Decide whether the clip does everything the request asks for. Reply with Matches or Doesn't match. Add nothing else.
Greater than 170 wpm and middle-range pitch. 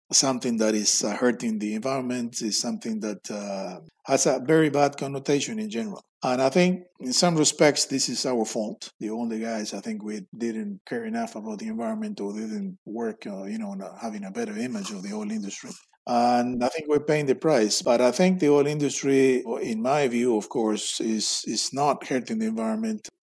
Matches